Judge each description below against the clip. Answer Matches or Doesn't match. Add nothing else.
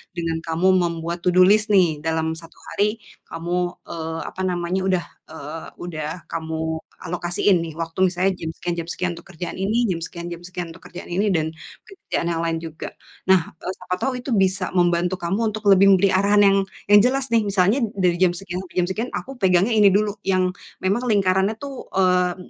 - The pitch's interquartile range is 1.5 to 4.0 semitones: Matches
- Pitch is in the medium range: Matches